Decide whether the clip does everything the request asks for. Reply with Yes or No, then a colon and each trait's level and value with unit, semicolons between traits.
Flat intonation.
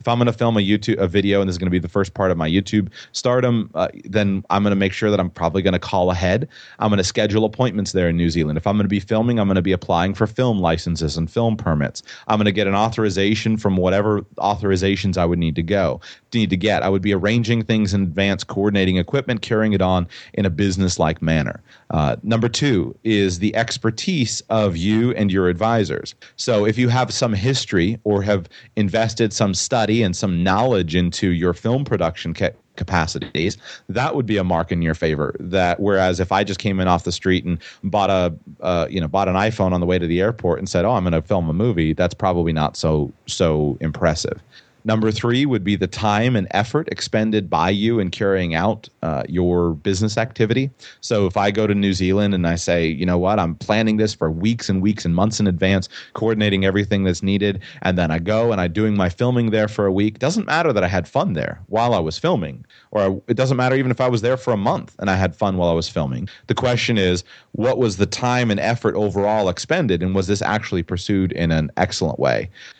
No: average, 3.4 semitones